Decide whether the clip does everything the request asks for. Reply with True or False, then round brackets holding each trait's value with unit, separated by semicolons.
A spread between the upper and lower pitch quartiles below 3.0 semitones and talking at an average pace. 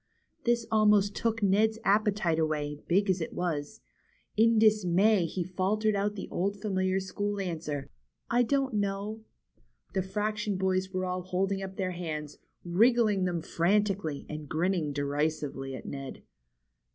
False (3.6 semitones; 145 wpm)